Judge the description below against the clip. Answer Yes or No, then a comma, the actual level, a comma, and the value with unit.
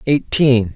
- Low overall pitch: Yes, low, 125 Hz